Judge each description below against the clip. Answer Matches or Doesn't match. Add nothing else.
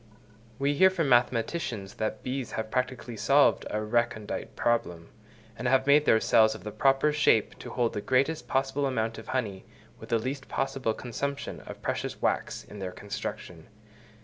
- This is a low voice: Matches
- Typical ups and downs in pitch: Matches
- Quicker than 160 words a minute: Matches